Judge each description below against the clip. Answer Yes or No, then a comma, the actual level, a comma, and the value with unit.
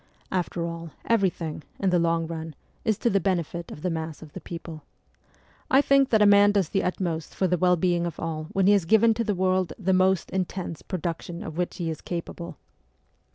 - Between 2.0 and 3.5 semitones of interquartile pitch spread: Yes, narrow, 2.6 semitones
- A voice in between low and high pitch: Yes, medium, 180 Hz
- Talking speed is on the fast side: Yes, fast, 210 wpm